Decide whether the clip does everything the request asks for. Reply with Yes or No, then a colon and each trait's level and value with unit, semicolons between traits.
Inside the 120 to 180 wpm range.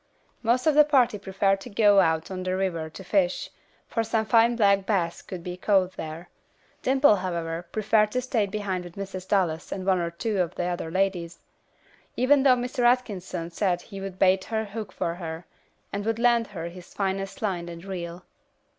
No: average, 190 wpm